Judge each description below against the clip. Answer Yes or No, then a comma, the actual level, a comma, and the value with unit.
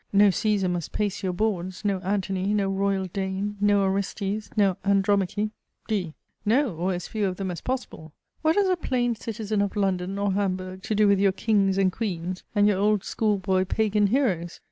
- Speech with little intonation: Yes, narrow, 2.0 semitones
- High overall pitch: Yes, high, 200 Hz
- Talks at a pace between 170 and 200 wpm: Yes, average, 190 wpm